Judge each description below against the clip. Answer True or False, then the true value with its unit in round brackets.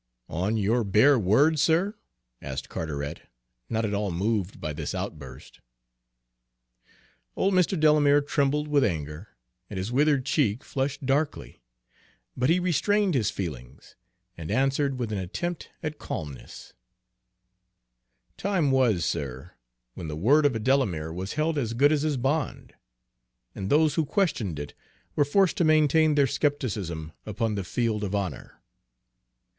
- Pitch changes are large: True (7.8 semitones)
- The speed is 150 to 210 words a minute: False (140 wpm)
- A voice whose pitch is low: True (125 Hz)